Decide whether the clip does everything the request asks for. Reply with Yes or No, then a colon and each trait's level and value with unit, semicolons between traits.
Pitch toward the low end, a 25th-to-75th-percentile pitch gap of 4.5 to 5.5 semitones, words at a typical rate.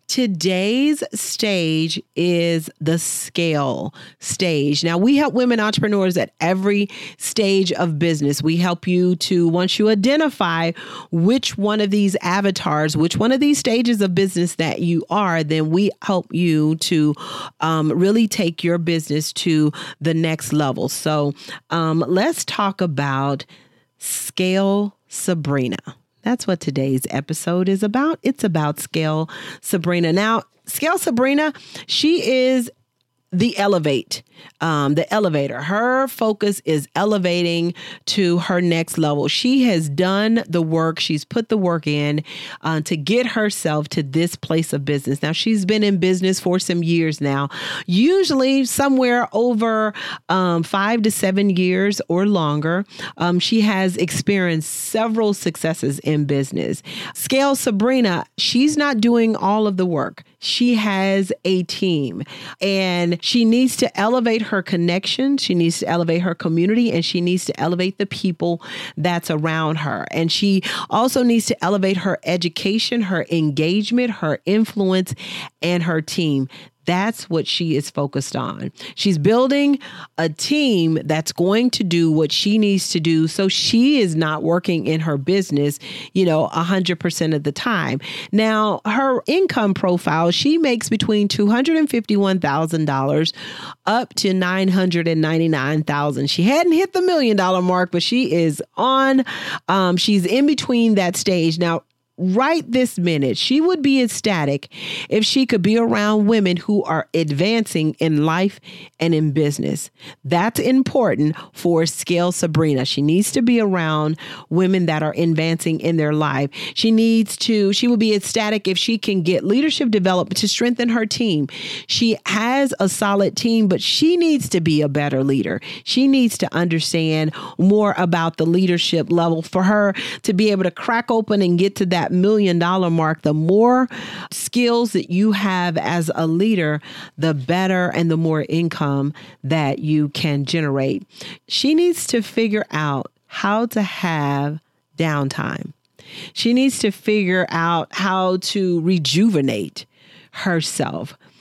No: medium, 185 Hz; average, 5.1 semitones; average, 150 wpm